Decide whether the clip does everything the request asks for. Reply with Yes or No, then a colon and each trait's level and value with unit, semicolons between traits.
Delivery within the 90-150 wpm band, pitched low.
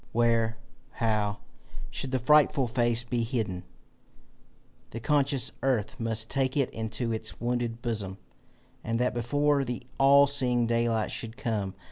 Yes: slow, 135 wpm; low, 120 Hz